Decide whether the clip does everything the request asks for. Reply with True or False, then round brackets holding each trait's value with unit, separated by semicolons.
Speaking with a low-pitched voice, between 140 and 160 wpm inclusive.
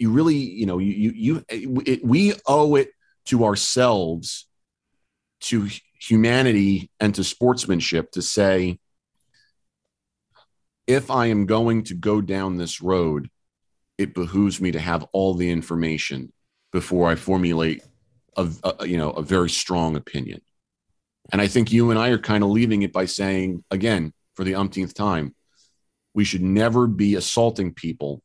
True (100 Hz; 155 wpm)